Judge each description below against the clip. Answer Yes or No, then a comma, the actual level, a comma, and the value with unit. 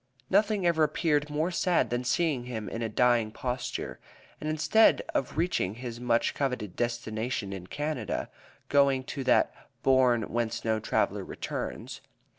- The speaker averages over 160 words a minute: No, average, 145 wpm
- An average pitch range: Yes, average, 4.6 semitones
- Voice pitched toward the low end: Yes, low, 125 Hz